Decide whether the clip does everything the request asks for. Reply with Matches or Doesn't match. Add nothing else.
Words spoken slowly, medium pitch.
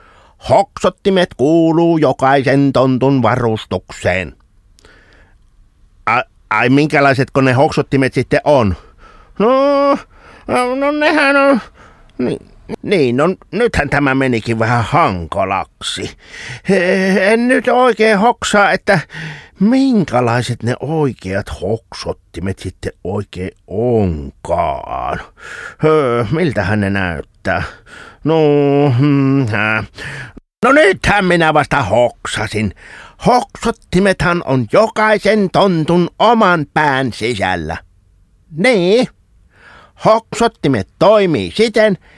Matches